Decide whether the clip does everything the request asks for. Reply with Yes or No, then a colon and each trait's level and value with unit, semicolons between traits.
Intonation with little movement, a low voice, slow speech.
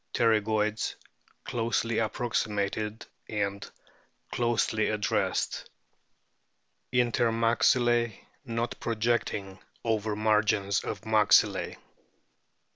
Yes: narrow, 1.8 semitones; low, 110 Hz; slow, 70 wpm